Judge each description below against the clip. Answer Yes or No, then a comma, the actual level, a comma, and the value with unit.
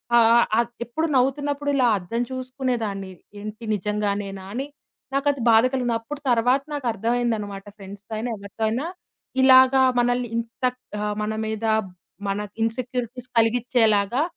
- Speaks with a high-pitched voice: Yes, high, 235 Hz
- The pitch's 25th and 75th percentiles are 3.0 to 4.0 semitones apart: Yes, average, 3.4 semitones